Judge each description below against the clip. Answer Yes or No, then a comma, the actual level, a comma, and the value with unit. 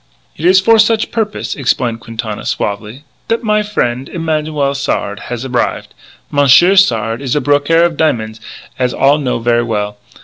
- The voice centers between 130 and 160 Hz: Yes, medium, 140 Hz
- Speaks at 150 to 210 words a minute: Yes, average, 160 wpm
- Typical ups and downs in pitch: No, wide, 6.1 semitones